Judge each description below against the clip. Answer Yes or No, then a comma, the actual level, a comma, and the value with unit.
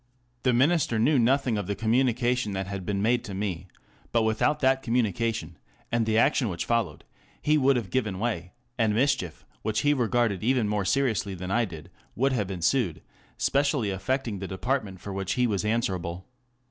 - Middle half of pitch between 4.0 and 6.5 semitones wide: Yes, average, 4.5 semitones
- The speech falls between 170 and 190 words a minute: Yes, average, 180 wpm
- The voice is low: Yes, low, 110 Hz